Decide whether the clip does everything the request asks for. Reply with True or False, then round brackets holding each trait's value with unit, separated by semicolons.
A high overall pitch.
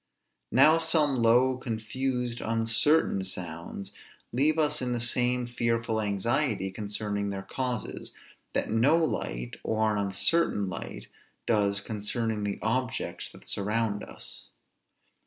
False (115 Hz)